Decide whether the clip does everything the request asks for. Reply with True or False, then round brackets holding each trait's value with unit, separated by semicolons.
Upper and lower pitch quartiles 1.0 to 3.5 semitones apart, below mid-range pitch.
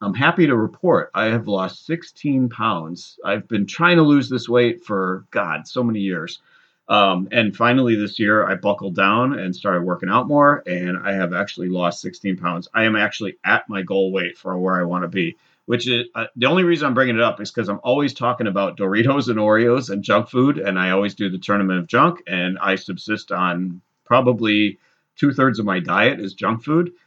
False (4.6 semitones; 105 Hz)